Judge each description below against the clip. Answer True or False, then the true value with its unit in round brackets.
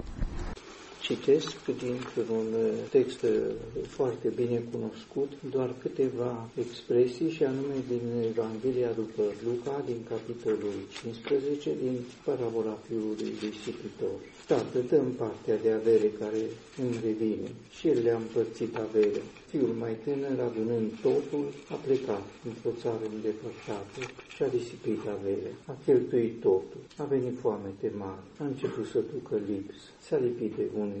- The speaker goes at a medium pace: True (130 wpm)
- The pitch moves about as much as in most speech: False (6.1 semitones)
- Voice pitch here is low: True (120 Hz)